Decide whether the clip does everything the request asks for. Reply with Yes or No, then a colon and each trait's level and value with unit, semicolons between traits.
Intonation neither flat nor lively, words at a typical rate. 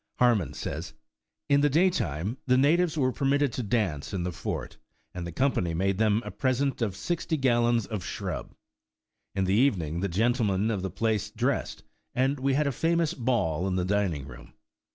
No: wide, 6.3 semitones; average, 180 wpm